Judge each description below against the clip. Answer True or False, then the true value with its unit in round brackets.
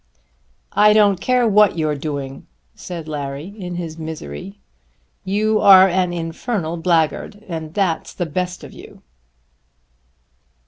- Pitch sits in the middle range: True (175 Hz)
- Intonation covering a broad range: False (4.1 semitones)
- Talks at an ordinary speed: False (125 wpm)